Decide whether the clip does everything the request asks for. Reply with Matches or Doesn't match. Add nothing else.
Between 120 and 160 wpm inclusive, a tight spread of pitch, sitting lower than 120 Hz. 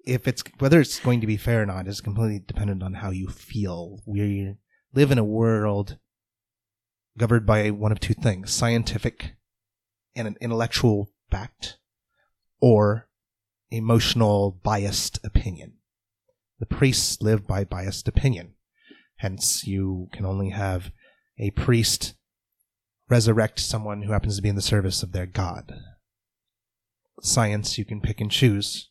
Matches